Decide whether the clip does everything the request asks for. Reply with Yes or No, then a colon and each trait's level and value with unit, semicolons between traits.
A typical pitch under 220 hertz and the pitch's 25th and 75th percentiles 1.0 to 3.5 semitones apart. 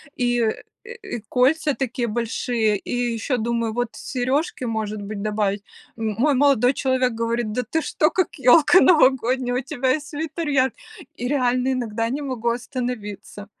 No: high, 245 Hz; average, 2.9 semitones